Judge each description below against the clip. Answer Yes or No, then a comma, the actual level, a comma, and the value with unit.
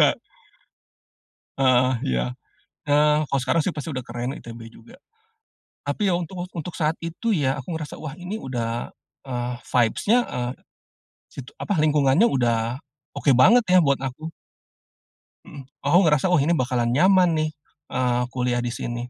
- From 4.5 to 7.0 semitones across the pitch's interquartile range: Yes, average, 5.0 semitones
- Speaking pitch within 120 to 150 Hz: Yes, medium, 140 Hz